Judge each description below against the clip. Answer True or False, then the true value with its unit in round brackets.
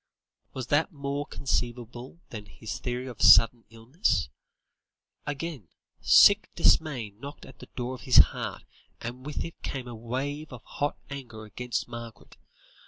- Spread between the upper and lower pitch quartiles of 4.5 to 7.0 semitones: False (3.3 semitones)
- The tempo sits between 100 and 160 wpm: True (145 wpm)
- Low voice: True (125 Hz)